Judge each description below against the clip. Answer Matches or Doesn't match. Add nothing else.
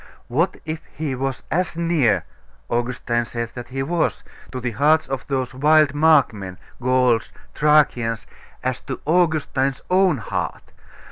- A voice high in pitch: Doesn't match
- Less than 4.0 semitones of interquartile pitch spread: Doesn't match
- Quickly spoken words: Doesn't match